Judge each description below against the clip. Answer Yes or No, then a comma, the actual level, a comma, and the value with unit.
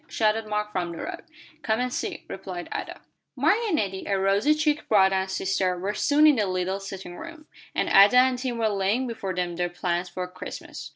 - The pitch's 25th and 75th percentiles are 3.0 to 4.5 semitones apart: No, average, 4.9 semitones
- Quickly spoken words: Yes, fast, 210 wpm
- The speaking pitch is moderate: No, high, 195 Hz